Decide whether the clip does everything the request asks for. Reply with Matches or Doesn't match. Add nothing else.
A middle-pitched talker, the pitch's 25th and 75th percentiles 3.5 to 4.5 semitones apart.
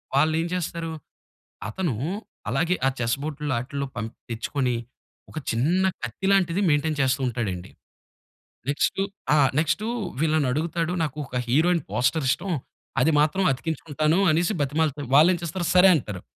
Matches